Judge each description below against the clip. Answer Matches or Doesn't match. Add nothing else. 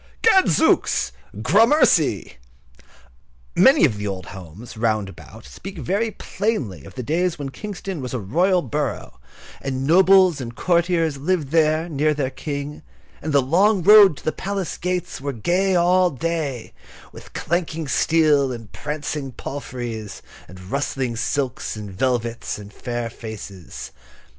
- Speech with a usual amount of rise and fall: Doesn't match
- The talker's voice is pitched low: Doesn't match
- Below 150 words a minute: Matches